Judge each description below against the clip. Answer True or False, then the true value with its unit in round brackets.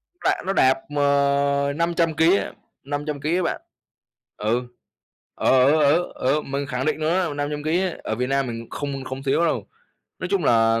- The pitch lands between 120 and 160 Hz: True (140 Hz)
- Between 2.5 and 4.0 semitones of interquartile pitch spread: True (3.3 semitones)